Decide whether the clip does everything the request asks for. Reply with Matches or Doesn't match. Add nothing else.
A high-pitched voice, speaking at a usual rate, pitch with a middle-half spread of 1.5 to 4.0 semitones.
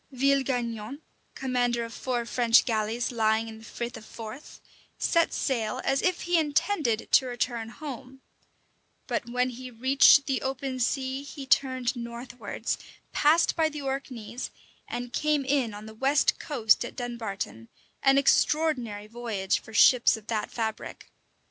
Matches